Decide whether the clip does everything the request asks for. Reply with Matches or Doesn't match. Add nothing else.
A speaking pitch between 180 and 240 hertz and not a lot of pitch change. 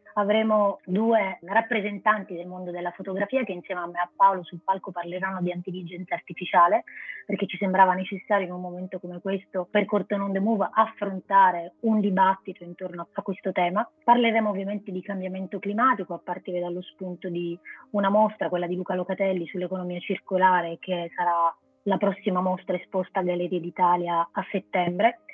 Matches